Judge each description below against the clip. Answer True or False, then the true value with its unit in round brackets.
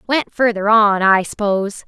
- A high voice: True (210 Hz)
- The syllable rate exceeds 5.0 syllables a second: False (4.1 syllables/s)